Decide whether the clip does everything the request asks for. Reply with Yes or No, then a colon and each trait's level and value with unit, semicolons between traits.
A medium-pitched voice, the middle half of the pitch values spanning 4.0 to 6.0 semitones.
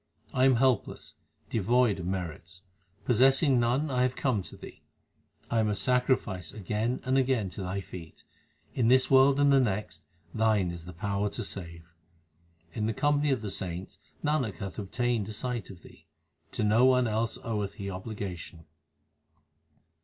No: low, 110 Hz; average, 5.0 semitones